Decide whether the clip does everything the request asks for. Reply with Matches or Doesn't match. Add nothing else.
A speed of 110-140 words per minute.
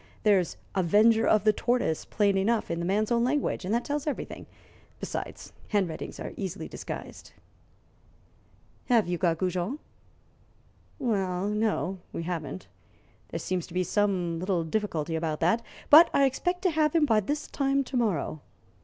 Doesn't match